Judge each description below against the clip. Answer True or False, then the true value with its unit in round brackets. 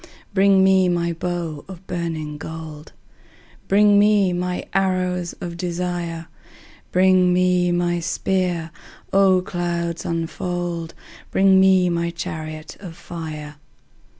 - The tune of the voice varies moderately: False (1.7 semitones)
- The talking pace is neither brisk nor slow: False (110 wpm)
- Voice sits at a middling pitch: True (175 Hz)